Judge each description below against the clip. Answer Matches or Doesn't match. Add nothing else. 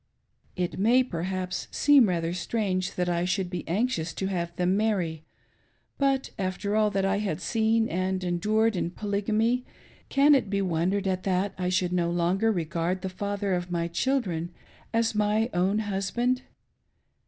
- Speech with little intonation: Doesn't match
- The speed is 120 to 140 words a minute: Doesn't match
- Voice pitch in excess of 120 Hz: Matches